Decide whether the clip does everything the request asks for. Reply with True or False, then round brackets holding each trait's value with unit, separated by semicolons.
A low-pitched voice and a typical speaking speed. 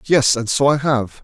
False (130 Hz; 240 wpm)